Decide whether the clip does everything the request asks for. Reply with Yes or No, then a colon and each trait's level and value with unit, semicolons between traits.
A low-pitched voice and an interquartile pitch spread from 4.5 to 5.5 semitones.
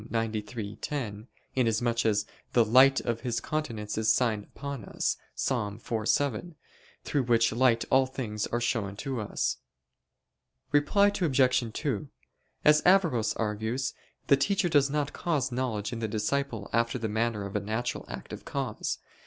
No: low, 120 Hz; average, 4.0 semitones